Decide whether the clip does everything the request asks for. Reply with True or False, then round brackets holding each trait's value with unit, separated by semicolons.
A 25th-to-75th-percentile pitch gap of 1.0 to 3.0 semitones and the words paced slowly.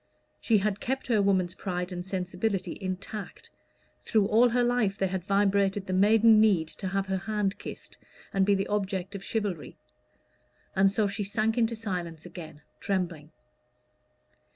False (2.4 semitones; 155 wpm)